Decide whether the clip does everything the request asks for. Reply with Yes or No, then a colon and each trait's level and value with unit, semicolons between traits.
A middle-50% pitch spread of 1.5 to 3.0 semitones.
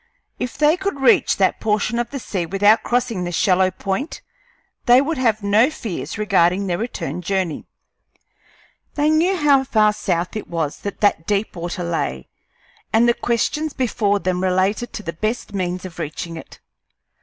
No: average, 5.1 semitones